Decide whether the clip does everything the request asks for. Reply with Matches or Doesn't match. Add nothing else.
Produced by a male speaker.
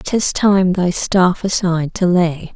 Doesn't match